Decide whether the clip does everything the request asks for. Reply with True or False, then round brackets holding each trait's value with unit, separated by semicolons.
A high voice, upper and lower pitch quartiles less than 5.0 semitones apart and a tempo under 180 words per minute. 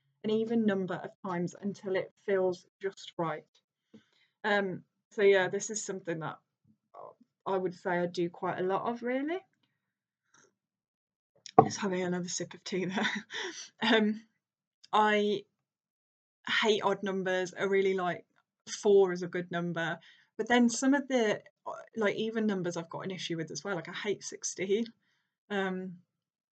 True (195 Hz; 3.3 semitones; 150 wpm)